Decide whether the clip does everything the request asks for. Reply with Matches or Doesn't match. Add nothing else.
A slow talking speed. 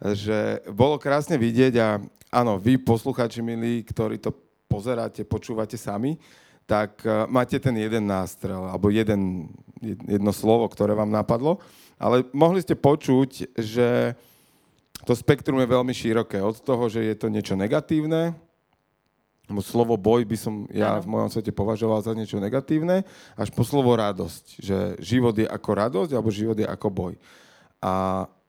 Doesn't match